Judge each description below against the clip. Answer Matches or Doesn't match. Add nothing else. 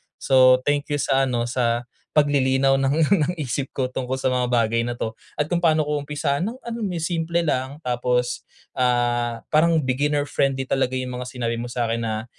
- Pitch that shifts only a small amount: Doesn't match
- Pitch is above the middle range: Doesn't match